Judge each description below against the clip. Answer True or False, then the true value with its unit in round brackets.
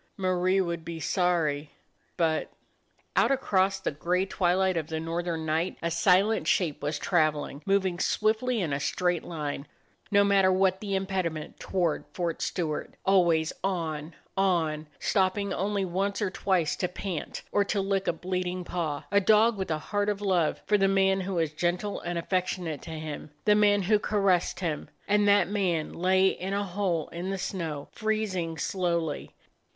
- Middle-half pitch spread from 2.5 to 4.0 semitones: True (2.9 semitones)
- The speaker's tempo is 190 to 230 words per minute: False (175 wpm)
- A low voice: False (185 Hz)